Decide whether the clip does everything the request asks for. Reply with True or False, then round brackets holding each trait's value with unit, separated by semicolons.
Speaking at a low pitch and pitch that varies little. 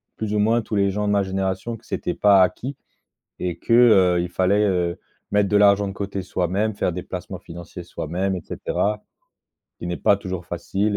True (100 Hz; 2.3 semitones)